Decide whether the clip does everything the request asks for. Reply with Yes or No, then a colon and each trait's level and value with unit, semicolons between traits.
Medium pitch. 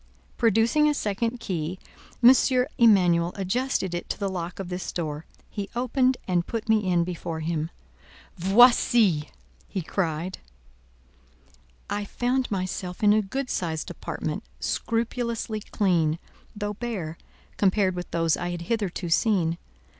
No: high, 195 Hz